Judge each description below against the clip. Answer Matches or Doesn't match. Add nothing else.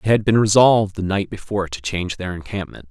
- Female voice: Doesn't match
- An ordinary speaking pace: Doesn't match